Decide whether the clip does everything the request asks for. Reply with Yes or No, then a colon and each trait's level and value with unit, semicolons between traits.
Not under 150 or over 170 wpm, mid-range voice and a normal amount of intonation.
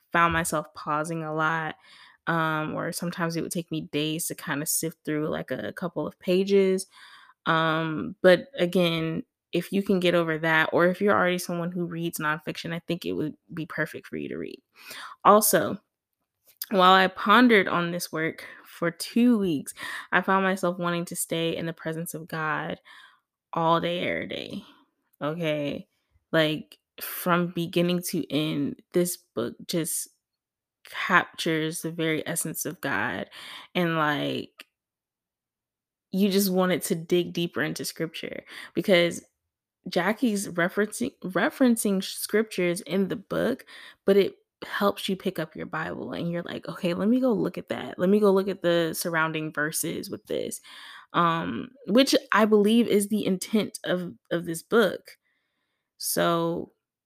Yes: average, 155 wpm; medium, 175 Hz; average, 3.2 semitones